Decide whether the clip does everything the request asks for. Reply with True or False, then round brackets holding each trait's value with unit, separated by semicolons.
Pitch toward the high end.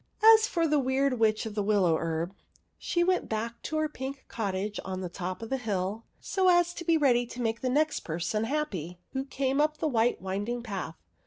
True (235 Hz)